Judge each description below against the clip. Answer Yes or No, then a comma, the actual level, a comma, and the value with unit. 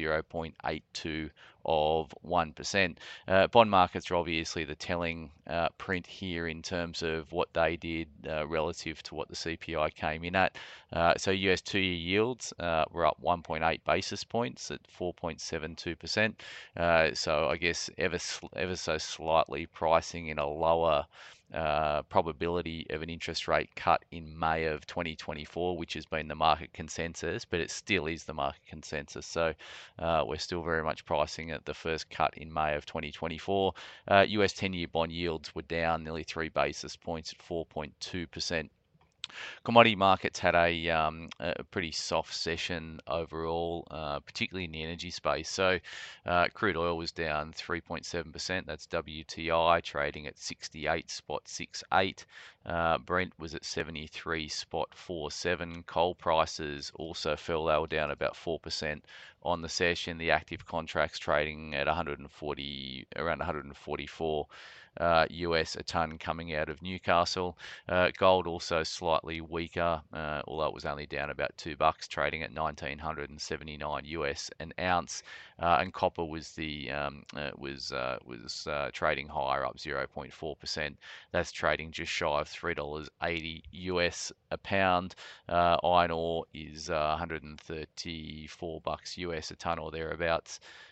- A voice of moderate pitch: No, very low, 80 Hz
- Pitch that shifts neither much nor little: No, narrow, 2.0 semitones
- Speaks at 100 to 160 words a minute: Yes, average, 150 wpm